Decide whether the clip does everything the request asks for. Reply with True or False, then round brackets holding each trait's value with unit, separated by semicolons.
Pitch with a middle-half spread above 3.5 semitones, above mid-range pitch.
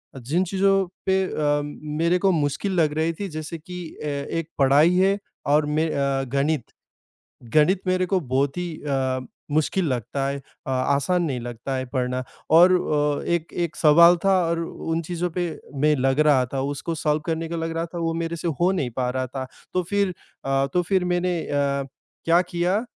False (4.1 semitones; 155 Hz)